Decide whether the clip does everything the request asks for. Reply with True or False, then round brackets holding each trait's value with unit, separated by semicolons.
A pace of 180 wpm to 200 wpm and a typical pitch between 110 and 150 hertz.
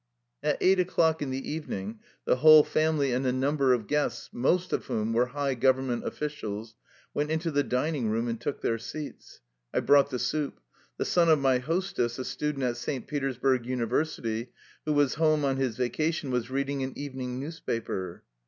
True (185 wpm; 135 Hz)